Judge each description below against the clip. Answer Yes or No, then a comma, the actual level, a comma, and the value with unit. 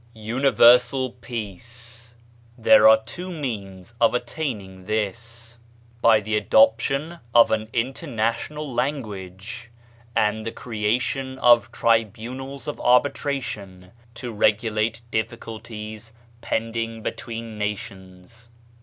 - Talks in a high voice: No, low, 115 Hz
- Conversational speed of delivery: No, slow, 90 wpm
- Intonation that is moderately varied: No, narrow, 2.3 semitones